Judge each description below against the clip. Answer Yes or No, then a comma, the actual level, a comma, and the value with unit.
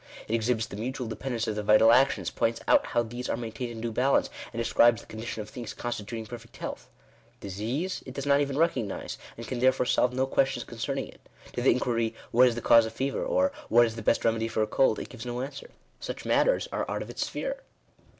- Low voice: Yes, low, 120 Hz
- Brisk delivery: Yes, fast, 235 wpm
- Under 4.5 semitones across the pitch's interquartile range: Yes, narrow, 2.5 semitones